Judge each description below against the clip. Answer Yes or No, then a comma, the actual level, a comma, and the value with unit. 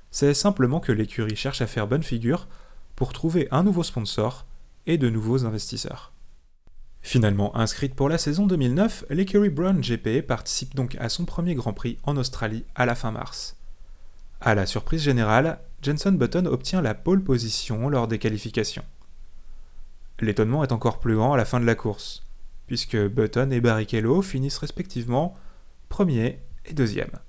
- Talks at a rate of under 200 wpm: Yes, average, 160 wpm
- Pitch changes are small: No, average, 4.9 semitones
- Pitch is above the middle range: No, low, 120 Hz